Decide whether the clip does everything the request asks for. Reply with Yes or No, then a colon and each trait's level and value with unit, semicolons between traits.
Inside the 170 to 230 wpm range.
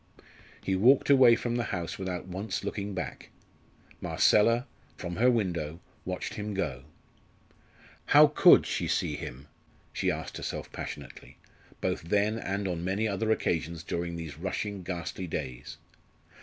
No: average, 140 wpm